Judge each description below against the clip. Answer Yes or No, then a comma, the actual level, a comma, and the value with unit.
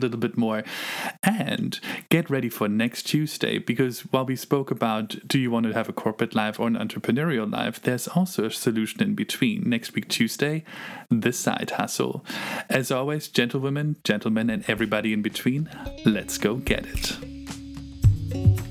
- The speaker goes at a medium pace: Yes, average, 165 wpm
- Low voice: Yes, low, 125 Hz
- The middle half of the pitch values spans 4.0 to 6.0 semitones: Yes, wide, 5.6 semitones